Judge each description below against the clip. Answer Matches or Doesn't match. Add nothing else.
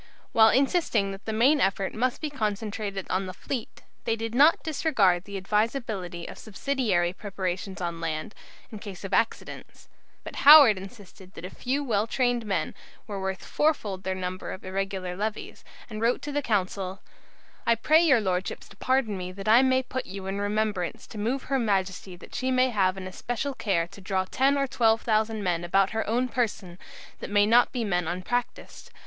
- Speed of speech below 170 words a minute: Doesn't match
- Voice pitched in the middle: Doesn't match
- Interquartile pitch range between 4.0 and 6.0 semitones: Matches